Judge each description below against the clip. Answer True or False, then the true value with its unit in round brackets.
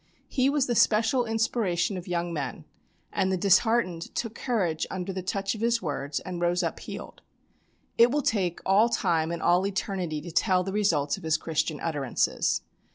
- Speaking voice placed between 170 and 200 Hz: True (185 Hz)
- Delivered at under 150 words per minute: False (180 wpm)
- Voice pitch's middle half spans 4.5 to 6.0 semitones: True (4.9 semitones)